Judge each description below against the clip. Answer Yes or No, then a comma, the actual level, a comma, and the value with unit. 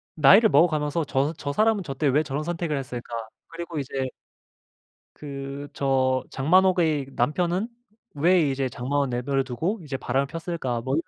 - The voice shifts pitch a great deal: No, average, 4.0 semitones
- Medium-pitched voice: Yes, medium, 145 Hz